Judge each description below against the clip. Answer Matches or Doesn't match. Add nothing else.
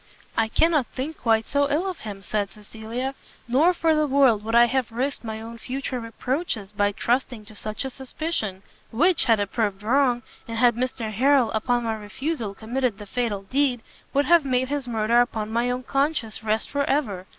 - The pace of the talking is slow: Doesn't match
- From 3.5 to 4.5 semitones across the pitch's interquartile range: Matches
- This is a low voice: Doesn't match